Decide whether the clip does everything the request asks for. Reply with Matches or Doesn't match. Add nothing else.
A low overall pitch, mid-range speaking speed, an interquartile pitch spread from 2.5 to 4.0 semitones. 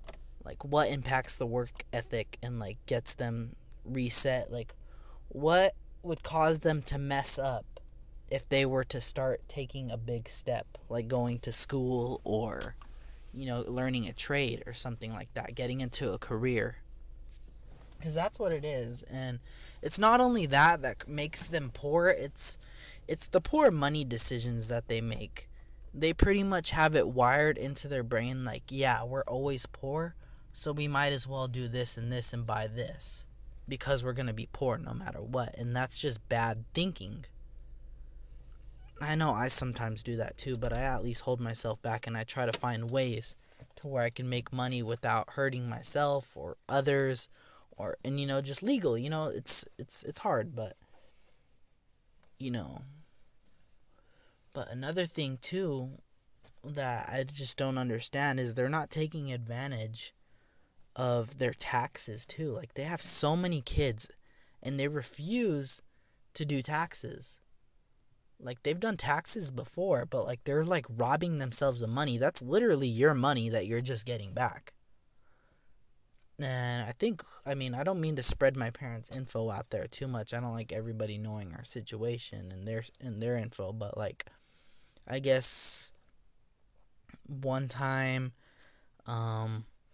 Matches